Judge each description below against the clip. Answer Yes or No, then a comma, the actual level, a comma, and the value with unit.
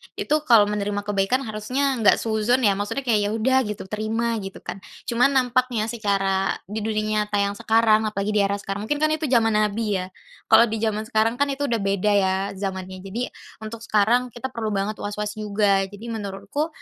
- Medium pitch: No, high, 215 Hz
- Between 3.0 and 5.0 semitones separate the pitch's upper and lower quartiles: No, narrow, 2.5 semitones